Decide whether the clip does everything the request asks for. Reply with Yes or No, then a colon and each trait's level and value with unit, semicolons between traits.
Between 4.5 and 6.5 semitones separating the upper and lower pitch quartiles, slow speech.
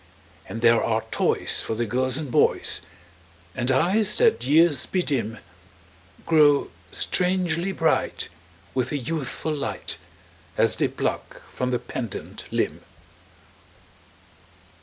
Yes: average, 5.3 semitones; slow, 115 wpm